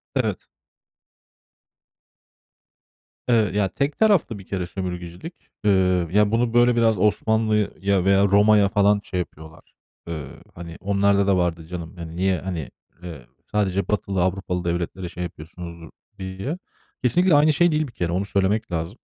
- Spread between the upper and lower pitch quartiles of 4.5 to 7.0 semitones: No, average, 3.4 semitones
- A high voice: No, very low, 95 Hz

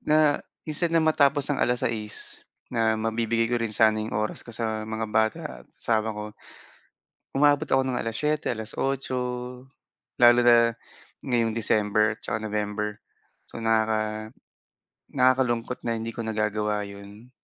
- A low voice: Yes, low, 115 Hz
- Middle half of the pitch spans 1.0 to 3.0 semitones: Yes, average, 2.7 semitones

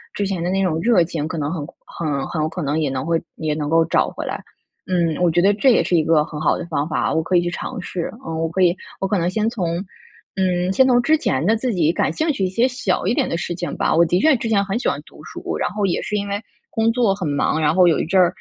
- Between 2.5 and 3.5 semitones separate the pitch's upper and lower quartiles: No, average, 3.9 semitones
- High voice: No, medium, 175 Hz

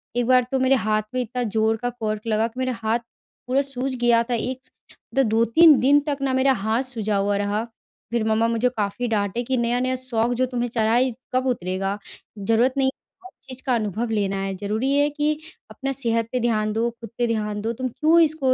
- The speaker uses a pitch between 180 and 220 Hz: No, high, 235 Hz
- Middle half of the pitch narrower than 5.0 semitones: Yes, average, 2.9 semitones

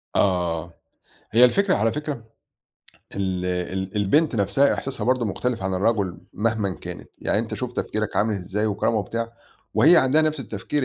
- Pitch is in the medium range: No, low, 110 Hz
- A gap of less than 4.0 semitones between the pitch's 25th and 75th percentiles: No, average, 4.8 semitones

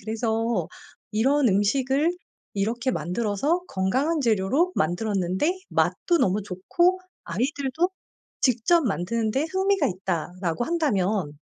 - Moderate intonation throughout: No, wide, 7.5 semitones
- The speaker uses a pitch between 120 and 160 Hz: No, high, 225 Hz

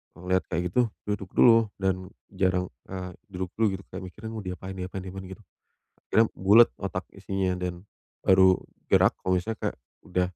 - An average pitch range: No, narrow, 1.5 semitones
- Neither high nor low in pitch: No, very low, 95 Hz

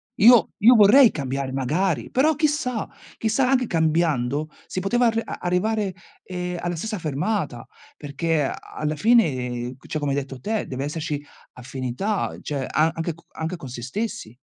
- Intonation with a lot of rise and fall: Yes, wide, 7.8 semitones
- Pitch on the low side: No, medium, 165 Hz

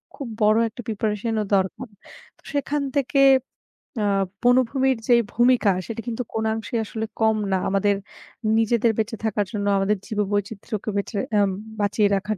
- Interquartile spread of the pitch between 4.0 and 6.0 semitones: No, average, 2.7 semitones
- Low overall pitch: No, high, 220 Hz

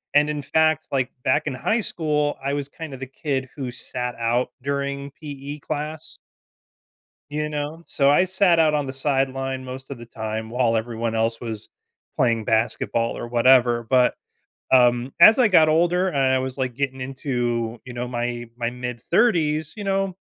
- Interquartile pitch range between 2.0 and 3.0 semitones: No, average, 3.8 semitones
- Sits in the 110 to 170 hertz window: Yes, low, 135 Hz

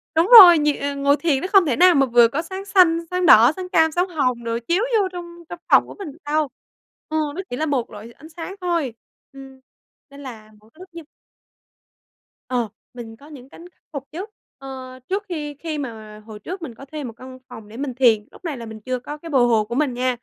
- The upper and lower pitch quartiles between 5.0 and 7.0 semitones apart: Yes, wide, 5.5 semitones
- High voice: Yes, very high, 280 Hz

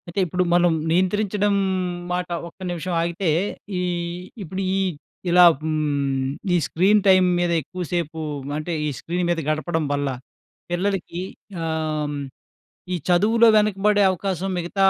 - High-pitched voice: No, medium, 175 Hz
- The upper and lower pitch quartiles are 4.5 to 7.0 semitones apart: No, average, 3.2 semitones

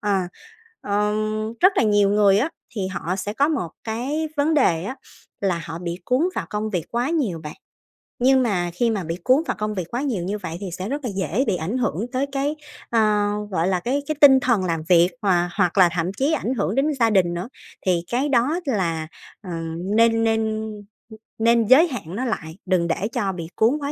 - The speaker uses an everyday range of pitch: No, wide, 5.8 semitones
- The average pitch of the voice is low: No, high, 210 Hz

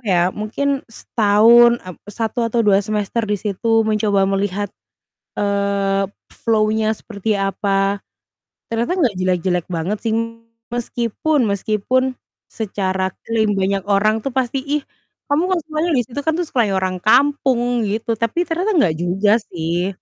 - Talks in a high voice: Yes, high, 215 Hz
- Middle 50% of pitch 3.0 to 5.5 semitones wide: Yes, average, 3.4 semitones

